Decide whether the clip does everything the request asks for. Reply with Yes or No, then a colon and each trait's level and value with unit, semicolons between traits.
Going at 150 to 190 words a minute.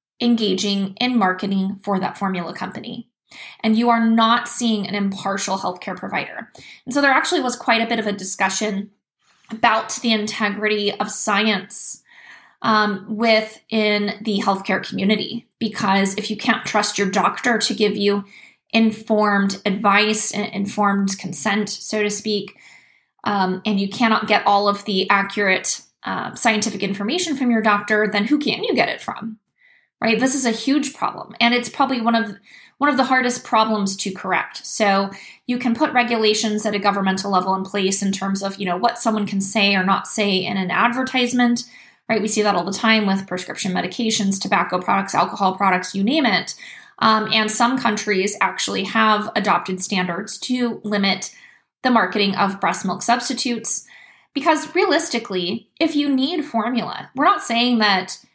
Yes: average, 170 wpm